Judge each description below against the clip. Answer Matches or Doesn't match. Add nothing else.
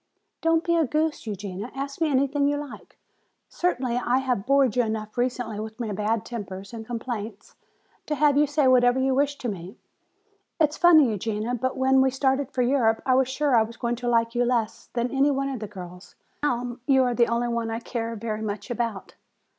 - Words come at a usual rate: Doesn't match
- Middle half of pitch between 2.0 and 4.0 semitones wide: Matches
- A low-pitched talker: Doesn't match